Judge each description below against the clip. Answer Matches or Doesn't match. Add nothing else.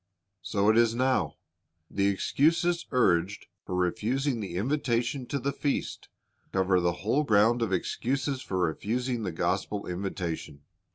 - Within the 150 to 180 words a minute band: Doesn't match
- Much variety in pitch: Matches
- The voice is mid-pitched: Doesn't match